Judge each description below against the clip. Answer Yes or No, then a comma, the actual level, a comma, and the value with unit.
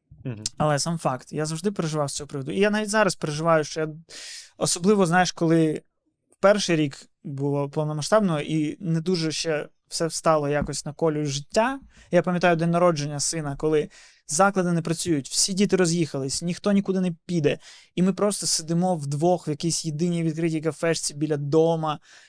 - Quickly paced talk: Yes, fast, 165 wpm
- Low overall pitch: No, medium, 165 Hz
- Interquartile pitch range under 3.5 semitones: Yes, average, 3.1 semitones